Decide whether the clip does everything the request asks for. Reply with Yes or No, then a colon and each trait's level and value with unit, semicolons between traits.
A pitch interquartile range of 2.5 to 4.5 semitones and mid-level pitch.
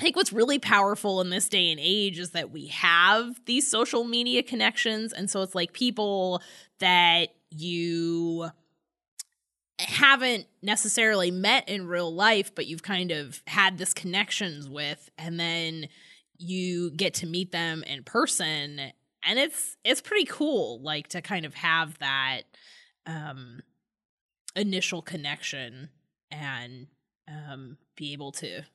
No: average, 5.1 semitones; medium, 175 Hz